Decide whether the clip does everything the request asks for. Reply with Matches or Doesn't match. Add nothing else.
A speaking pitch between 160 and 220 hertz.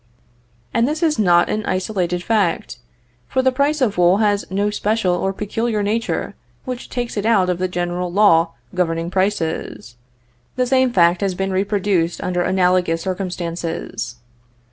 Matches